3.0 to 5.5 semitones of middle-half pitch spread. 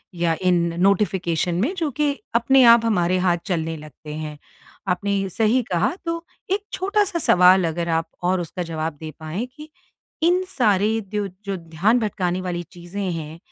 Yes: average, 5.1 semitones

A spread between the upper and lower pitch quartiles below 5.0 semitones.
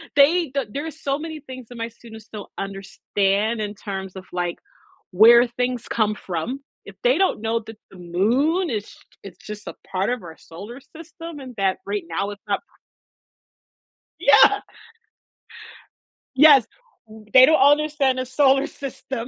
No: wide, 5.5 semitones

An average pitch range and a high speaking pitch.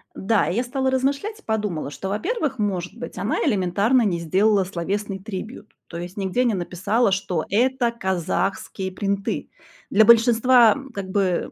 Yes: average, 4.1 semitones; high, 205 Hz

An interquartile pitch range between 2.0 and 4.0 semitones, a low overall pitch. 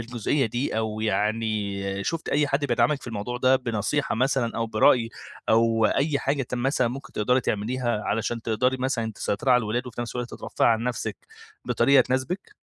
Yes: average, 2.9 semitones; low, 120 Hz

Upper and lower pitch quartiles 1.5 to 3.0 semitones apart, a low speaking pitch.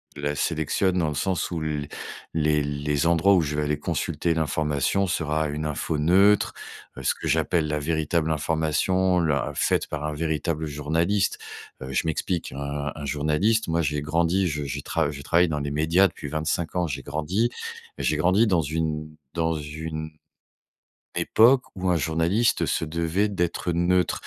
Yes: average, 2.7 semitones; very low, 80 Hz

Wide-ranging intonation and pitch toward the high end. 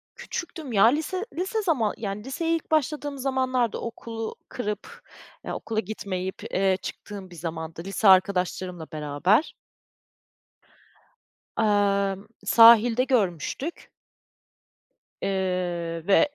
Yes: wide, 5.7 semitones; high, 210 Hz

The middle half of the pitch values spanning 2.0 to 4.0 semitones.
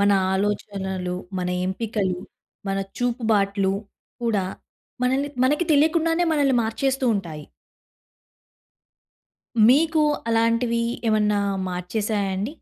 No: average, 5.1 semitones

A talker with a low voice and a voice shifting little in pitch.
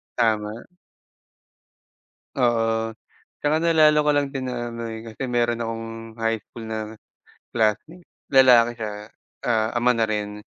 Yes: low, 115 Hz; narrow, 2.2 semitones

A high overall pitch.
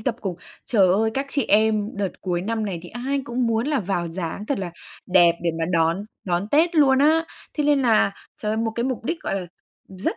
Yes: high, 220 Hz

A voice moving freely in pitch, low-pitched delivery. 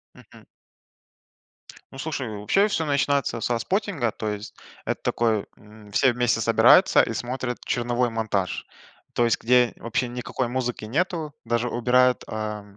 No: average, 2.7 semitones; low, 120 Hz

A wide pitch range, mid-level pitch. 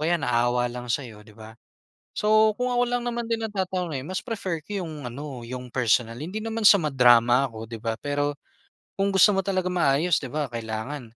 Yes: wide, 8.1 semitones; medium, 150 Hz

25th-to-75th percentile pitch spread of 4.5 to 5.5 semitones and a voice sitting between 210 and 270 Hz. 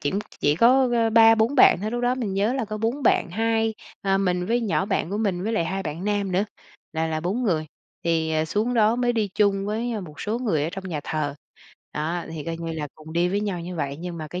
No: average, 5.2 semitones; high, 195 Hz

